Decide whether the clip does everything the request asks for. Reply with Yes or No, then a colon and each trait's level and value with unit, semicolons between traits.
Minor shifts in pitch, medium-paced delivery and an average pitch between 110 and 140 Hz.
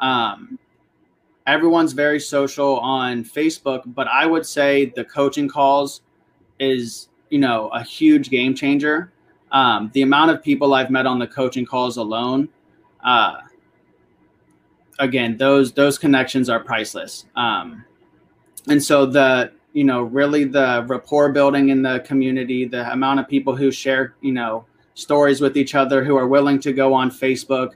Yes: narrow, 1.6 semitones; average, 155 wpm; low, 135 Hz